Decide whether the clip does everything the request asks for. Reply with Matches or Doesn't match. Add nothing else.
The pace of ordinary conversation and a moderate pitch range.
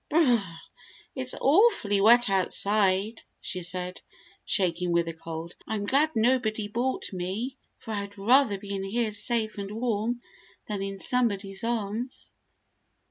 Matches